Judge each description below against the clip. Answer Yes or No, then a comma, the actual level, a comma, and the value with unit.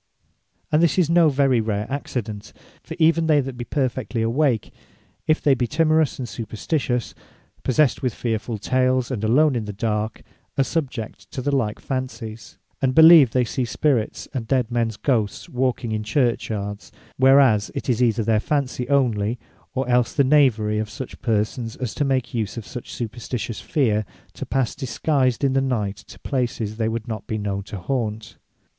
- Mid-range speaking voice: No, low, 125 Hz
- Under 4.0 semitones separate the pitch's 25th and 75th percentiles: Yes, average, 3.6 semitones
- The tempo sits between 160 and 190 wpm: Yes, average, 175 wpm